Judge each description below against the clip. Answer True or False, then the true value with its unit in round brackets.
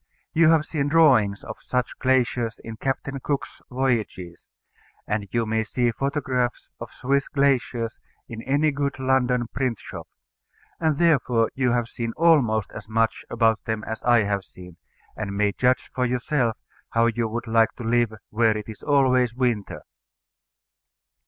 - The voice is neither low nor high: False (120 Hz)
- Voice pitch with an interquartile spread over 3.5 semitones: False (3.0 semitones)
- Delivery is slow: False (155 wpm)